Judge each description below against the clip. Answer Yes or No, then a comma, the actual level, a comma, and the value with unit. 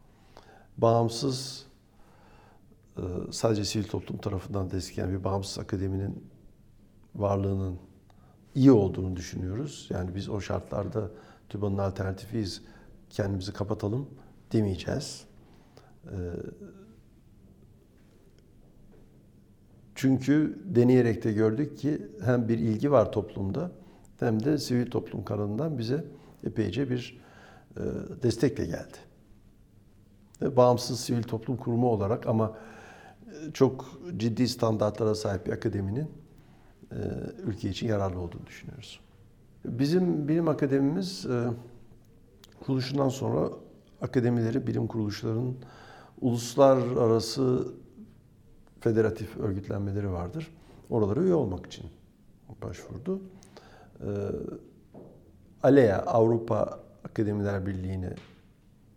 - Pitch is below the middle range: Yes, low, 110 Hz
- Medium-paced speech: No, slow, 80 wpm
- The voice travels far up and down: No, average, 3.9 semitones